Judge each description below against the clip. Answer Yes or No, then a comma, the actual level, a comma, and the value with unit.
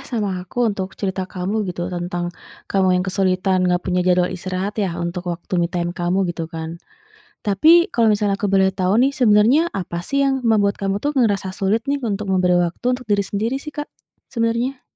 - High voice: Yes, high, 195 Hz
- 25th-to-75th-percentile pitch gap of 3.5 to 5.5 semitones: Yes, average, 3.8 semitones